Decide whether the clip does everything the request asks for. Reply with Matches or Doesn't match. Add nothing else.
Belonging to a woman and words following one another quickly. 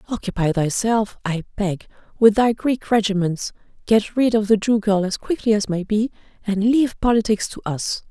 Doesn't match